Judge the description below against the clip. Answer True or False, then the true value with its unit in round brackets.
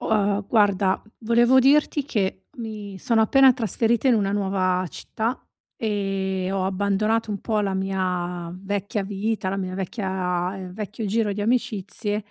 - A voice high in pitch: True (200 Hz)